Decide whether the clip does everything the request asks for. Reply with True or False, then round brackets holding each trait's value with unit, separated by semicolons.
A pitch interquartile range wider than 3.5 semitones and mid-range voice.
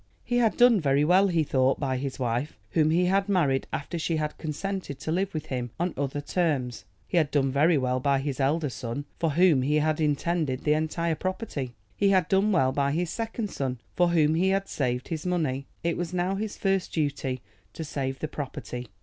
True (4.6 semitones; 155 Hz)